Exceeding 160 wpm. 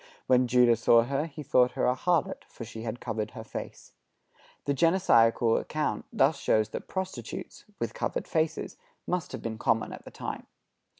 Yes: average, 175 wpm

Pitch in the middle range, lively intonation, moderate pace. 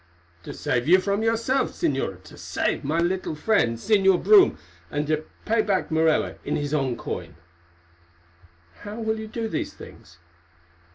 Yes: medium, 180 Hz; wide, 7.2 semitones; average, 155 wpm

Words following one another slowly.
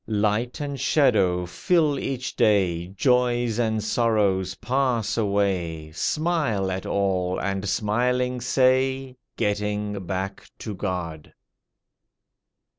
Yes: slow, 100 wpm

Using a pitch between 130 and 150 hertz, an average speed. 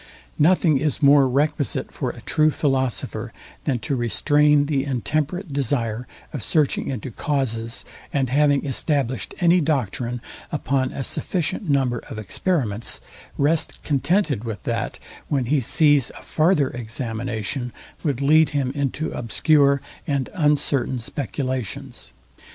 No: medium, 140 Hz; slow, 125 wpm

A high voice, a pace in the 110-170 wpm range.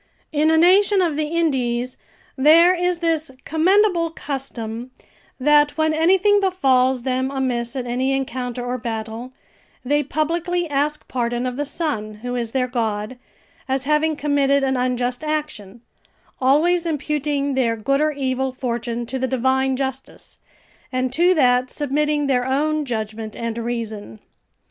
Yes: very high, 265 Hz; average, 145 wpm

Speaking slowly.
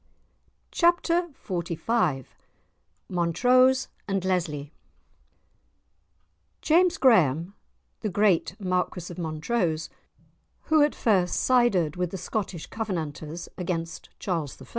Yes: slow, 95 wpm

